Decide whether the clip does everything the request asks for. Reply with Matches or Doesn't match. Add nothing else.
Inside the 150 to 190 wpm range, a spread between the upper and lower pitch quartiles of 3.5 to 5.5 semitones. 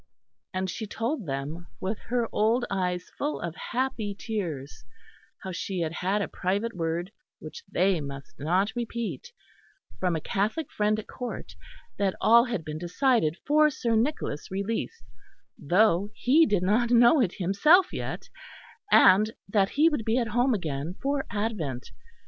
Matches